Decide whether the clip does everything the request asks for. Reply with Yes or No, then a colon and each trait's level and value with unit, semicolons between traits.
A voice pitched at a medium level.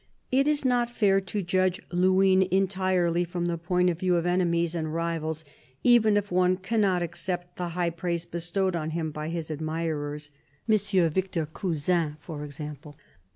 Yes: medium, 175 Hz